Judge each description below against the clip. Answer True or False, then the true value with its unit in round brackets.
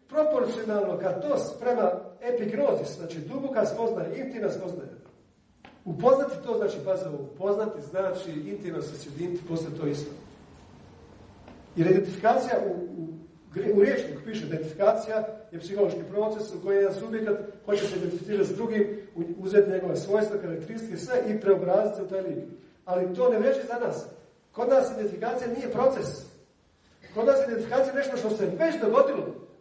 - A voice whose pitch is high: True (205 Hz)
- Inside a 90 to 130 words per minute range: False (150 wpm)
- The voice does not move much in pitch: False (4.1 semitones)